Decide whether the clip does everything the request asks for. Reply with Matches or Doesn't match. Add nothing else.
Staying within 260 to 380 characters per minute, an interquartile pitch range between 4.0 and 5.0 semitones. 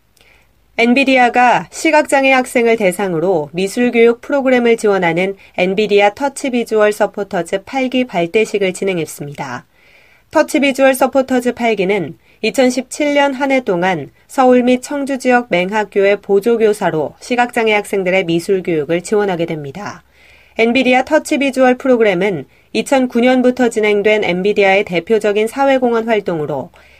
Matches